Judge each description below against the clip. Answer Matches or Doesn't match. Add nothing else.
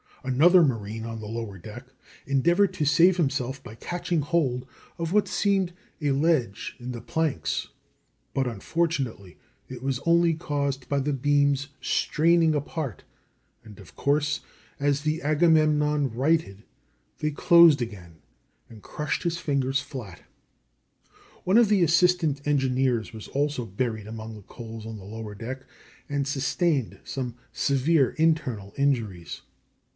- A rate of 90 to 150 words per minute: Matches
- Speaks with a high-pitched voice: Doesn't match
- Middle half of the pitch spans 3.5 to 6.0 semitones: Matches